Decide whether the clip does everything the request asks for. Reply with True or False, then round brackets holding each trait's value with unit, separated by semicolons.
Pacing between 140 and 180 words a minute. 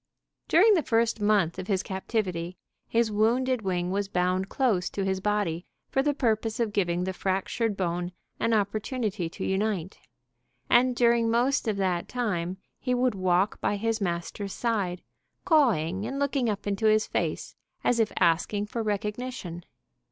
True (160 wpm)